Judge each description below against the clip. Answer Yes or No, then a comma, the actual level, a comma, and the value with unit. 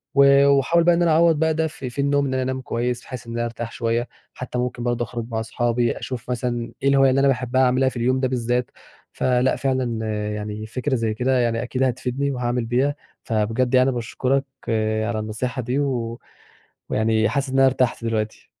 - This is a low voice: Yes, low, 125 Hz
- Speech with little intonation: Yes, narrow, 2.2 semitones